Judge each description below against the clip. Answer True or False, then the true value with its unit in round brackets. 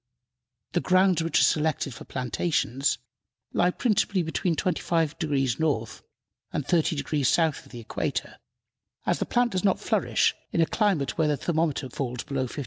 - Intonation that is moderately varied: True (4.2 semitones)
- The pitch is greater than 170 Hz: False (160 Hz)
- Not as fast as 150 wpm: False (155 wpm)